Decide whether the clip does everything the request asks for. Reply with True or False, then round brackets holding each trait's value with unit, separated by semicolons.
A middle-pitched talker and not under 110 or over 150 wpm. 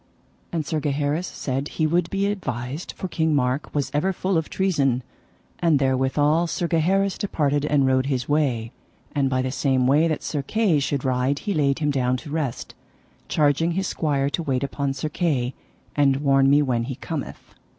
False (145 Hz; 185 wpm)